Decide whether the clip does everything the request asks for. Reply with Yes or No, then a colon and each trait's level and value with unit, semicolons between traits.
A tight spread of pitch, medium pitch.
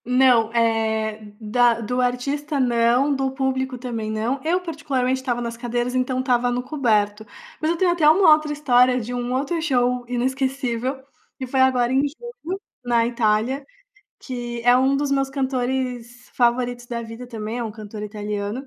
No: narrow, 2.3 semitones; very high, 250 Hz